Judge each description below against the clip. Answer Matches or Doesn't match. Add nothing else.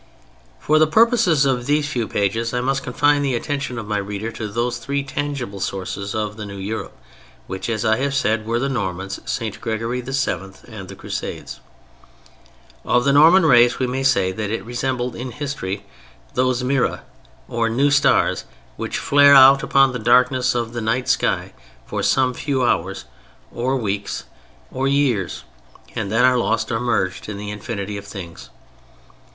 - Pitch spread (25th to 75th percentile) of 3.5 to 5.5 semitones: Matches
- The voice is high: Doesn't match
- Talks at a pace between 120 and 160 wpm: Doesn't match